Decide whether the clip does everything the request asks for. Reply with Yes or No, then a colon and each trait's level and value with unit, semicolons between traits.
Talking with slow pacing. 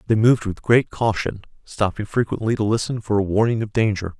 No: average, 200 wpm